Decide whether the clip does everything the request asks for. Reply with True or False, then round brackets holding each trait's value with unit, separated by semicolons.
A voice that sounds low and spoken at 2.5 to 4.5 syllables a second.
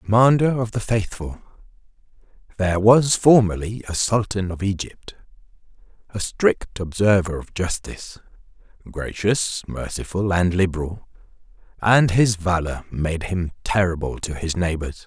True (100 Hz; 4.4 syllables/s)